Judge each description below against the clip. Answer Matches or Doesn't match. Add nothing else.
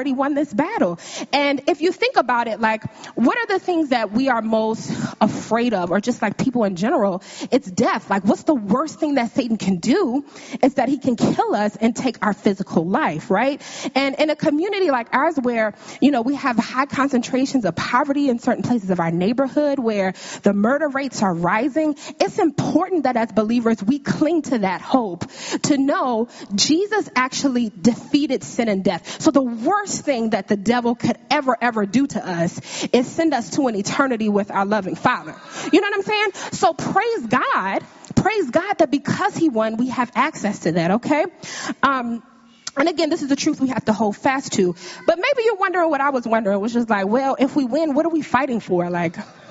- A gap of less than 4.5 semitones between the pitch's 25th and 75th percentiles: Doesn't match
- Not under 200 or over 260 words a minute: Matches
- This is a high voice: Matches